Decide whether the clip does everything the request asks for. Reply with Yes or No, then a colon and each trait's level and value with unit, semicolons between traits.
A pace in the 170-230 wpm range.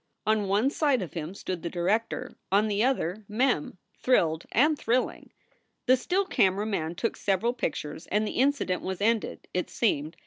Yes: average, 175 wpm